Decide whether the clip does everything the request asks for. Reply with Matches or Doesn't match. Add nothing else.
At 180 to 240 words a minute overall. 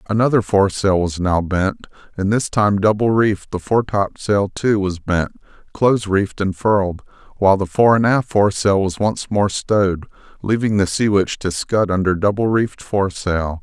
Doesn't match